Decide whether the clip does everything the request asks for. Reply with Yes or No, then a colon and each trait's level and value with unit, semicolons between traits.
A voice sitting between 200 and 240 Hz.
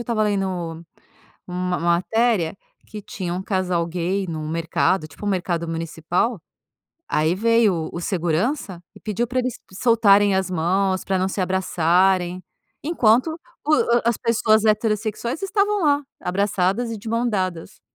No: high, 190 Hz